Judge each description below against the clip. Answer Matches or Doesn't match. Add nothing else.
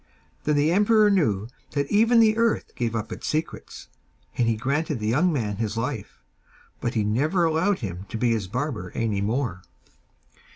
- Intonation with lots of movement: Matches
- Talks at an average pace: Matches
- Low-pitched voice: Matches